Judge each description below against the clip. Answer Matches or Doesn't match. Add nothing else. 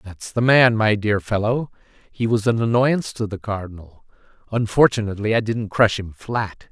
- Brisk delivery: Doesn't match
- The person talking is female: Doesn't match